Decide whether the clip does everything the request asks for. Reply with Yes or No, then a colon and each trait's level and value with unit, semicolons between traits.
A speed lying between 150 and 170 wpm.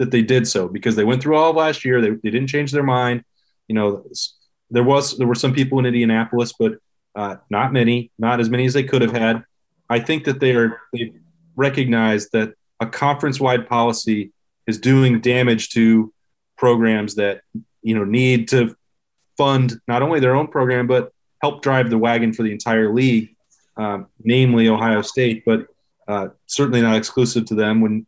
No: average, 190 wpm